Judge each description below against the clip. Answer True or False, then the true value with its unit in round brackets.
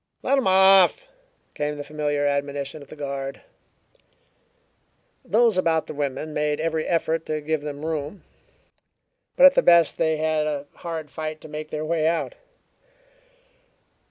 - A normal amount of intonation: False (2.1 semitones)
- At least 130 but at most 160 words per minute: True (150 wpm)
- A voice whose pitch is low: False (155 Hz)